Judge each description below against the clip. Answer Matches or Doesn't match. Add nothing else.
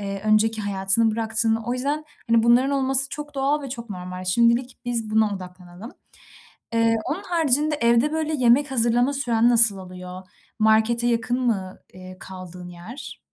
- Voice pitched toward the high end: Matches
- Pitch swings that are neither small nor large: Matches